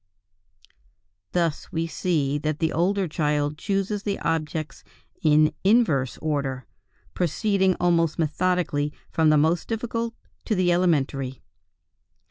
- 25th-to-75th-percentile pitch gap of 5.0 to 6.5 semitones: No, average, 3.7 semitones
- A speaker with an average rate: No, slow, 110 wpm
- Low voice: No, medium, 165 Hz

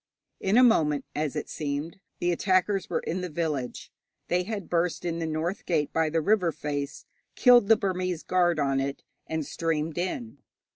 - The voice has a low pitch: No, medium, 170 Hz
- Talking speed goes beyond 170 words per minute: Yes, average, 180 wpm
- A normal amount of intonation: Yes, average, 3.5 semitones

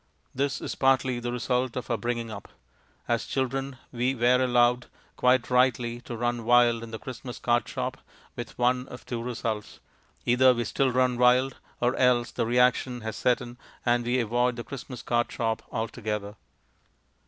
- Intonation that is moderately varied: No, narrow, 1.1 semitones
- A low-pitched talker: Yes, low, 120 Hz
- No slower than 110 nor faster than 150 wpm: No, average, 170 wpm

